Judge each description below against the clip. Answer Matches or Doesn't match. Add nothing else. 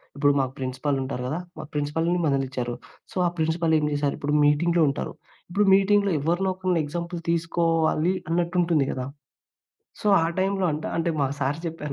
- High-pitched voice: Doesn't match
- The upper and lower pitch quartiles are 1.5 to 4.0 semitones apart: Matches